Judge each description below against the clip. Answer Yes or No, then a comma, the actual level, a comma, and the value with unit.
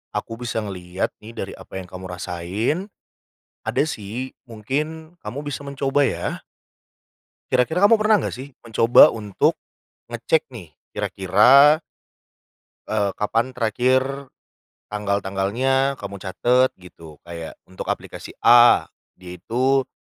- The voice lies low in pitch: Yes, low, 115 Hz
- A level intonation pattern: No, wide, 5.5 semitones